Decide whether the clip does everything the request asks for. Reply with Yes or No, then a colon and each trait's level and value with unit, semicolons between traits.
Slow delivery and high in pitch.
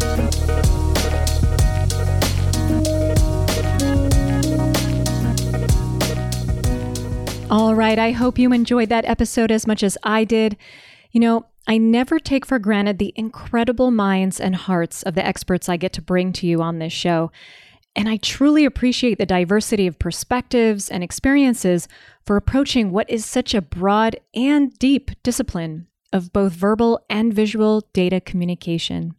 Yes: slow, 130 wpm; high, 195 Hz